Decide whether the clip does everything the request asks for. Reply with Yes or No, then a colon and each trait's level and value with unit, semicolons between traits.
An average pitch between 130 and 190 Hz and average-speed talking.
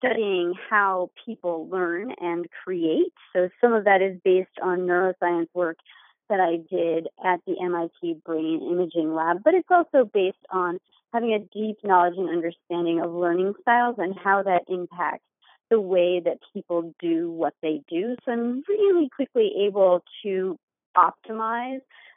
Yes: medium, 185 Hz; average, 155 wpm